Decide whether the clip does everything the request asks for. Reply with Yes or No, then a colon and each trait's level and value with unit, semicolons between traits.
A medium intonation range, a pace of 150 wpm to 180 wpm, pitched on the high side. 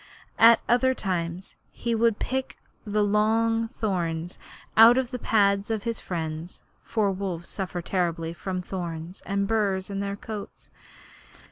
No: average, 4.0 semitones; average, 140 wpm; high, 200 Hz